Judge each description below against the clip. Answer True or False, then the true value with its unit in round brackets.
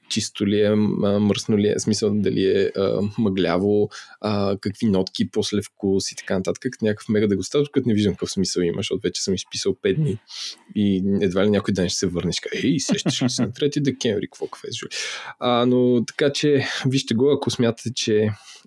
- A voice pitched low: True (105 Hz)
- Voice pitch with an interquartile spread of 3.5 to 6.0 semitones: True (4.1 semitones)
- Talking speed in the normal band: False (205 wpm)